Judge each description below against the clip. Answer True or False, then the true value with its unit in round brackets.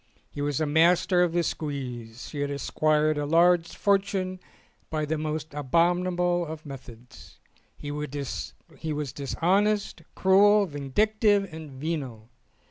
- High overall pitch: False (155 Hz)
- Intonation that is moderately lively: True (3.7 semitones)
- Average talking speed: False (125 wpm)